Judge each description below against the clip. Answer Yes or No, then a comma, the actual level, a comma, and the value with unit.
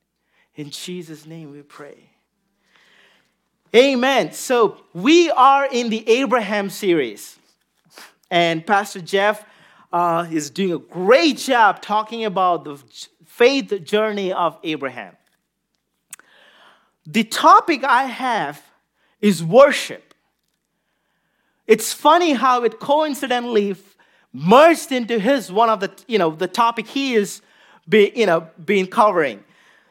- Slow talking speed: Yes, slow, 110 wpm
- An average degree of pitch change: No, wide, 5.9 semitones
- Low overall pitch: No, high, 215 Hz